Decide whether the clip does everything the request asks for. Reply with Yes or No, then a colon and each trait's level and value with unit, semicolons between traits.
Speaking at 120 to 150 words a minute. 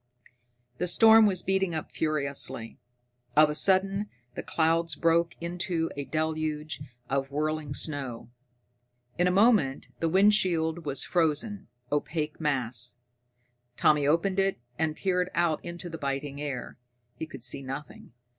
Yes: slow, 135 wpm